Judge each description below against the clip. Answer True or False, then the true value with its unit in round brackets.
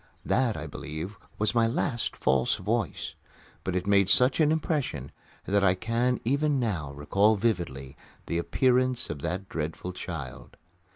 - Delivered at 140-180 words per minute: True (150 wpm)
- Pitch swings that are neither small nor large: False (7.1 semitones)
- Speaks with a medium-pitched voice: False (100 Hz)